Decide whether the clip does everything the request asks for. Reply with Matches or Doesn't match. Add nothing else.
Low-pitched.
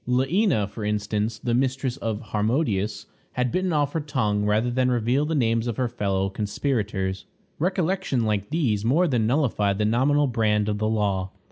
Matches